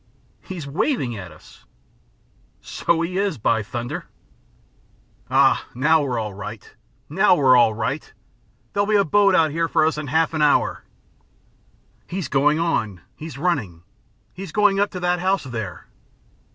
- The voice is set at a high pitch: No, medium, 155 Hz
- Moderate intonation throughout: No, wide, 7.0 semitones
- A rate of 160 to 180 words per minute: No, average, 150 wpm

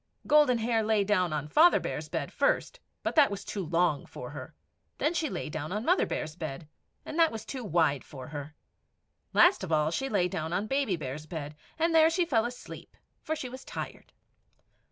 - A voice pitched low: No, high, 205 Hz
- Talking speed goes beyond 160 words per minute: Yes, average, 200 wpm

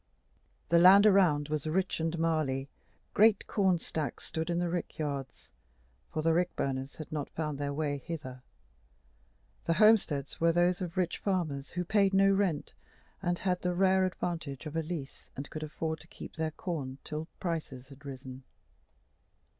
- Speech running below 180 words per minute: Yes, average, 170 wpm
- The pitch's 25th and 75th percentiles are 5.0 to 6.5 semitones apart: No, average, 3.7 semitones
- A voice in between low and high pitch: Yes, medium, 160 Hz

